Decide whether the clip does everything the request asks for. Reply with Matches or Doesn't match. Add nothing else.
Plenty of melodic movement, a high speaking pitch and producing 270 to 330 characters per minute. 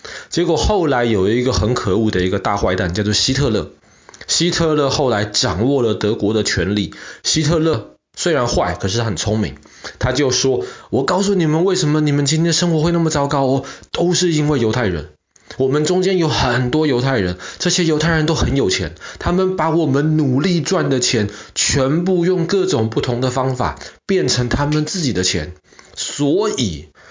Doesn't match